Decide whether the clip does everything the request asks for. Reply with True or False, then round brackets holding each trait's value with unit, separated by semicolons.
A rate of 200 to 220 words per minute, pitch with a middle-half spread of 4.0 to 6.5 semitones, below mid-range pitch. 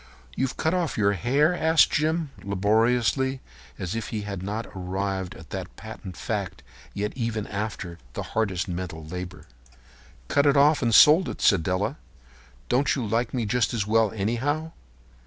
False (160 wpm; 5.5 semitones; 110 Hz)